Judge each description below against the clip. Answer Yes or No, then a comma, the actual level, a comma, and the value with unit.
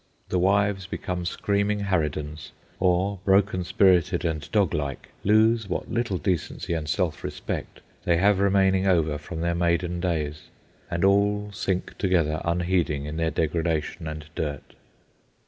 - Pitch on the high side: No, very low, 90 Hz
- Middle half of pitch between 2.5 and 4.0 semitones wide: Yes, average, 3.4 semitones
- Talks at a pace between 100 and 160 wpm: Yes, slow, 135 wpm